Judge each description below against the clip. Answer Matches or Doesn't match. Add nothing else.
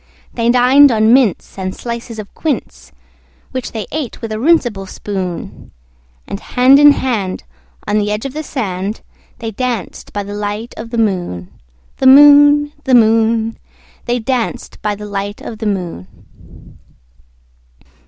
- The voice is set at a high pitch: Matches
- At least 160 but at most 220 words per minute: Doesn't match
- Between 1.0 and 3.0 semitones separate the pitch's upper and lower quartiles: Doesn't match